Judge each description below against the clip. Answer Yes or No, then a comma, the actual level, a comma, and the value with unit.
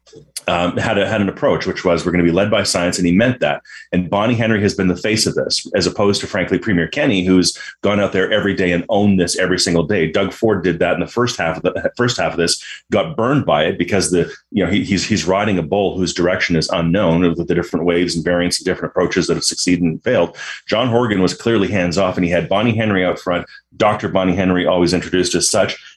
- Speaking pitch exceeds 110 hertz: No, very low, 90 Hz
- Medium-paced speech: No, fast, 260 wpm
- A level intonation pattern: Yes, narrow, 2.3 semitones